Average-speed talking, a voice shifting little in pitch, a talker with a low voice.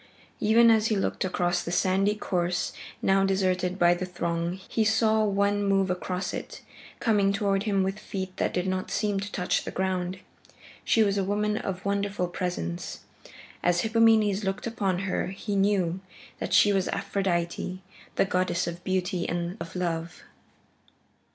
No: average, 160 wpm; narrow, 2.2 semitones; high, 190 Hz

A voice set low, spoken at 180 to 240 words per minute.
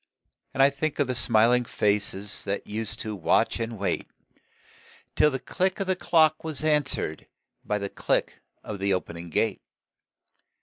No: low, 115 Hz; average, 160 wpm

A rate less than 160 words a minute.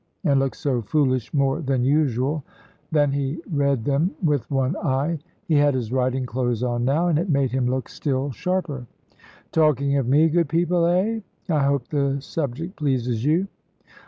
No: average, 170 wpm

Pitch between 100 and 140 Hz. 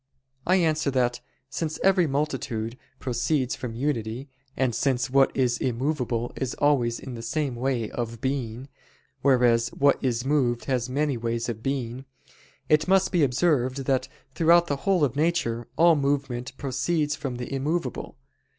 Yes: low, 135 Hz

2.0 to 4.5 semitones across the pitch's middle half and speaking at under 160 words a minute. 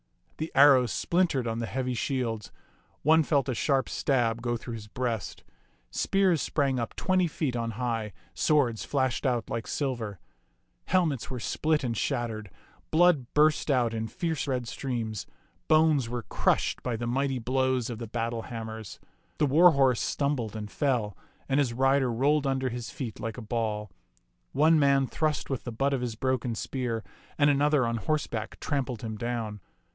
No: average, 3.6 semitones; average, 170 wpm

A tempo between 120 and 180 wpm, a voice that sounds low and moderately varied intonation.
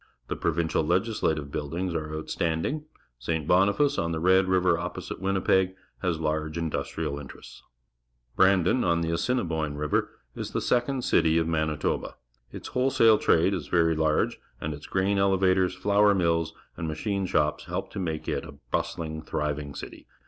Yes: average, 165 wpm; very low, 85 Hz; average, 3.5 semitones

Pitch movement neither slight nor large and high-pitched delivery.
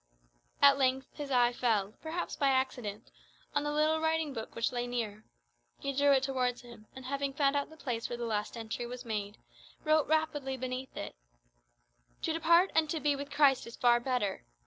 Yes: average, 3.5 semitones; very high, 265 Hz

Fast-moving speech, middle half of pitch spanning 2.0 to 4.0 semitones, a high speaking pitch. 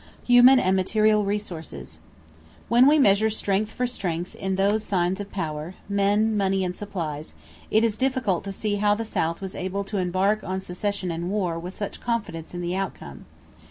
No: average, 180 wpm; average, 2.9 semitones; high, 195 Hz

